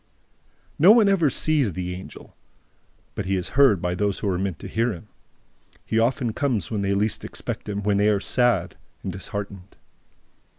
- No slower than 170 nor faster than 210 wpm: Yes, average, 180 wpm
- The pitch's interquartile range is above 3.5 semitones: Yes, average, 4.1 semitones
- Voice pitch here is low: Yes, low, 105 Hz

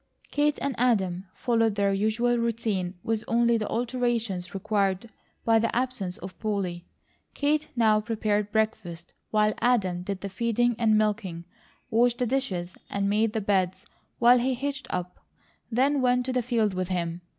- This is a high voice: Yes, high, 220 Hz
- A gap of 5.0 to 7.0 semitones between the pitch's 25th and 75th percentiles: No, average, 3.9 semitones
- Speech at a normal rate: Yes, average, 160 wpm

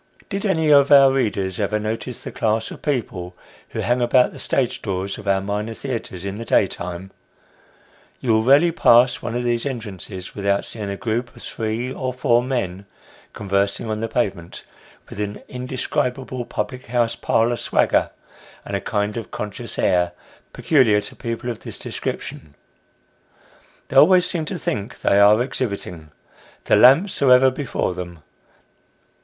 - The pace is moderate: Yes, average, 160 wpm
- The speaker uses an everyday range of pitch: Yes, average, 4.2 semitones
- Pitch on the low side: Yes, low, 115 Hz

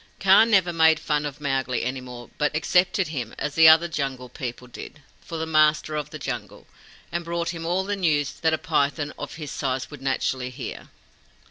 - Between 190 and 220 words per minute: Yes, average, 200 wpm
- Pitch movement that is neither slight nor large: Yes, average, 3.7 semitones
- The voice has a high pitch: No, medium, 150 Hz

